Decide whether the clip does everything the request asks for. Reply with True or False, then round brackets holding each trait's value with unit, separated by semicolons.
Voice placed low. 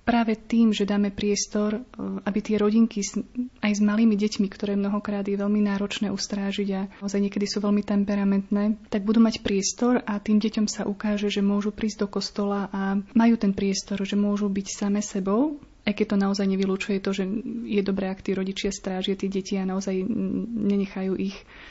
False (205 Hz)